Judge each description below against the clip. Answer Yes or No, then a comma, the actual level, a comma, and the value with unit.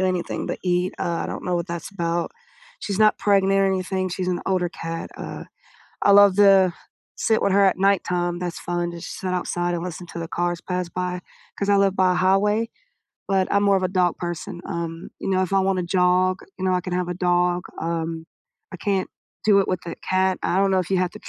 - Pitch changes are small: Yes, narrow, 1.7 semitones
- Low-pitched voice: No, medium, 180 Hz